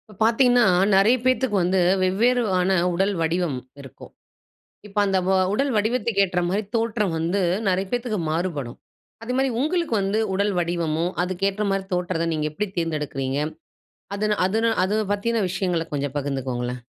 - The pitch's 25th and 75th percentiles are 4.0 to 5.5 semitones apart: Yes, average, 4.6 semitones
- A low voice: No, high, 190 Hz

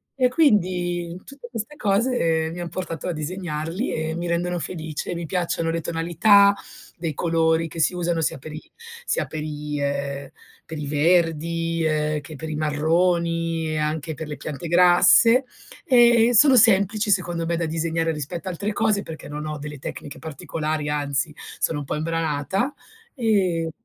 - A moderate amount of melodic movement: Yes, average, 3.0 semitones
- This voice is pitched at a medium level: Yes, medium, 165 Hz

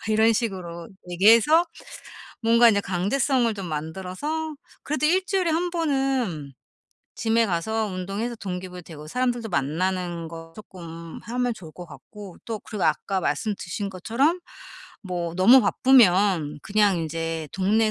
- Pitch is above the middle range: Yes, high, 200 Hz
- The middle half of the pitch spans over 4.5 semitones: Yes, wide, 5.5 semitones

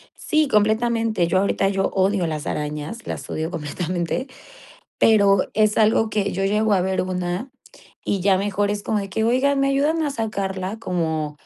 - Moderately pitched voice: No, high, 200 Hz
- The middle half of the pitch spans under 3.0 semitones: No, average, 3.4 semitones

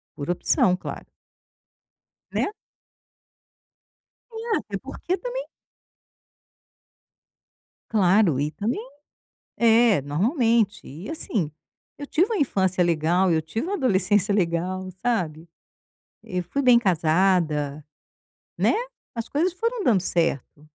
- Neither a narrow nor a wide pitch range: No, wide, 6.3 semitones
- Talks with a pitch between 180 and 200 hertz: Yes, high, 190 Hz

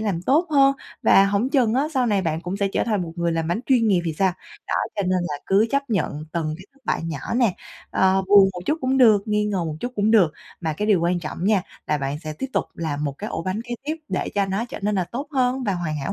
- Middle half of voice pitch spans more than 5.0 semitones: Yes, wide, 5.6 semitones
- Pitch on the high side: Yes, high, 195 Hz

